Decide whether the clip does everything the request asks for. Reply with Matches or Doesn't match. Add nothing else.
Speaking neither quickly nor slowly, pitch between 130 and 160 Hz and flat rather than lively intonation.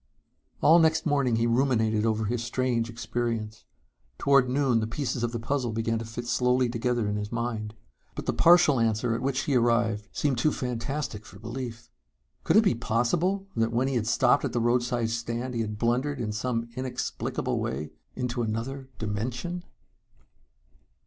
Doesn't match